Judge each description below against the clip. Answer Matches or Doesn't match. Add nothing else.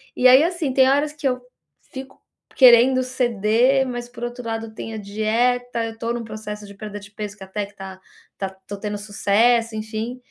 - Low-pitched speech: Doesn't match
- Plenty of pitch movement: Doesn't match